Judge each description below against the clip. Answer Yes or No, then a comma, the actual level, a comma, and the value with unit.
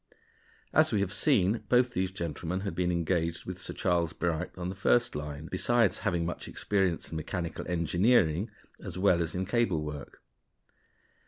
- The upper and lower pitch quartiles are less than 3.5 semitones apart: Yes, average, 2.7 semitones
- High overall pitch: No, very low, 90 Hz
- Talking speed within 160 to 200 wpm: Yes, average, 165 wpm